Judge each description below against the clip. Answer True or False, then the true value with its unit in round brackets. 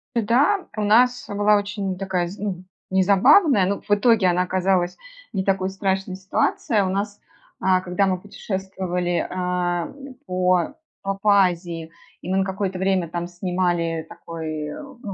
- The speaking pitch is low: False (190 Hz)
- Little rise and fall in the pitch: True (2.2 semitones)